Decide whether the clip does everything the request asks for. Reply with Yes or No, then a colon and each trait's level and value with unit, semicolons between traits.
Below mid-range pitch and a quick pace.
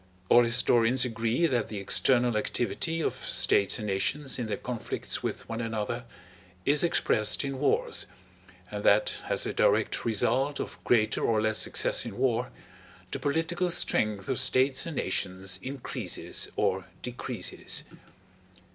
No: low, 120 Hz; average, 140 wpm